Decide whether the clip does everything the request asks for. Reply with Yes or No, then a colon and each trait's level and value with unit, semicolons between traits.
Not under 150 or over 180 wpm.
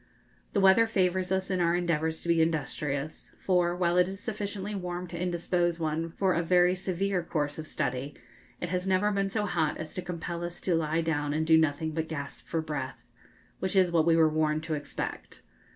No: fast, 205 wpm